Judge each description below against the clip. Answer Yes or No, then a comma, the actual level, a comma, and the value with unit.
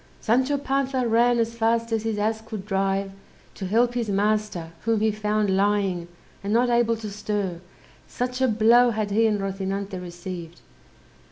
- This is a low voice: No, high, 215 Hz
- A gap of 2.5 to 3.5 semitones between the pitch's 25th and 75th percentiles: Yes, average, 2.9 semitones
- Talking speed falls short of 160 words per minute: No, average, 165 wpm